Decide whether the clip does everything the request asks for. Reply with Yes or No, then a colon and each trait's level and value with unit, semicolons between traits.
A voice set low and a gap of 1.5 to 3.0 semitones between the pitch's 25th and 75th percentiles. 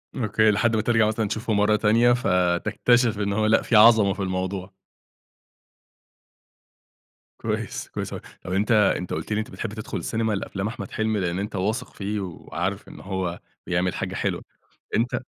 Yes: low, 105 Hz; average, 2.7 semitones